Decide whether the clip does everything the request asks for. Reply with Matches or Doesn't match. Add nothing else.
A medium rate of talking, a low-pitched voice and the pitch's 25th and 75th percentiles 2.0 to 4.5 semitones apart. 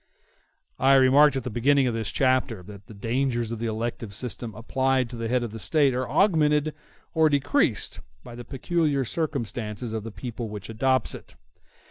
Matches